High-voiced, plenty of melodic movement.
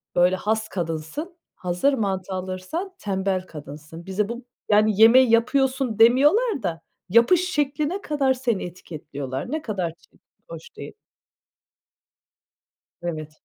Yes: high, 210 Hz; wide, 7.1 semitones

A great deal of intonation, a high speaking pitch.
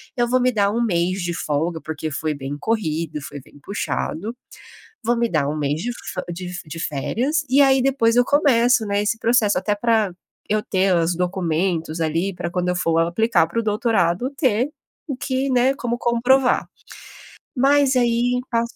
Yes: wide, 6.4 semitones; high, 210 Hz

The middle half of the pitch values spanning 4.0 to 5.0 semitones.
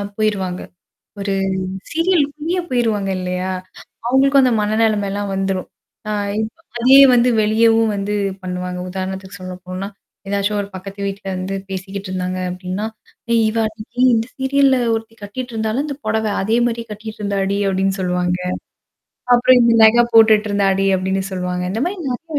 No: average, 3.4 semitones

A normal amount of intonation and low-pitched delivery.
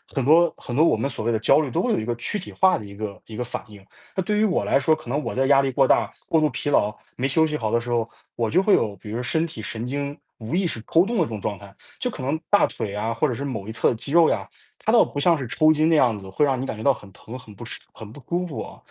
No: wide, 6.0 semitones; low, 130 Hz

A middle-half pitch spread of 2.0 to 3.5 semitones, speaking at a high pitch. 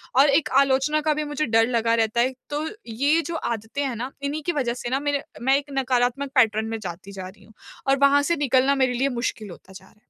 No: average, 3.9 semitones; very high, 260 Hz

